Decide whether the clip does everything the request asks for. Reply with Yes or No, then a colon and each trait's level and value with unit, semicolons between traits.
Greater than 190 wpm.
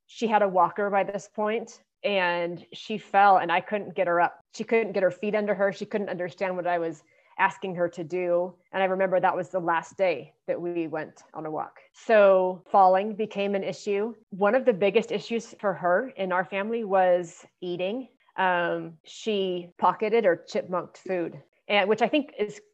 Yes: average, 200 wpm